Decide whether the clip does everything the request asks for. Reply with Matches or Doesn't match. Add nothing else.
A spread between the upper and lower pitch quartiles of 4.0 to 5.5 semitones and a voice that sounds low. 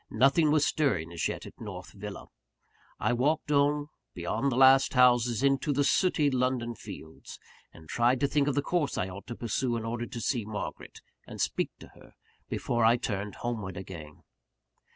Matches